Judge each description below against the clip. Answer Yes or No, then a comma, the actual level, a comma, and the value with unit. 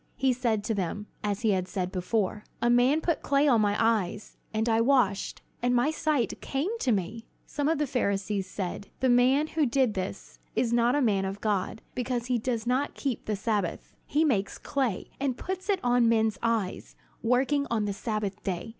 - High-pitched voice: Yes, high, 230 Hz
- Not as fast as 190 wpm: No, average, 200 wpm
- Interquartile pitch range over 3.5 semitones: Yes, average, 4.2 semitones